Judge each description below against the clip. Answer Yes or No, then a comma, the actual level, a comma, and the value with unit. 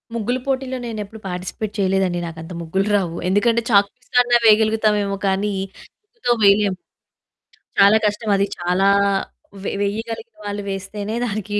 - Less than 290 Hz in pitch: Yes, high, 205 Hz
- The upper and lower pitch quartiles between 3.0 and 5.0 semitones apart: No, narrow, 2.4 semitones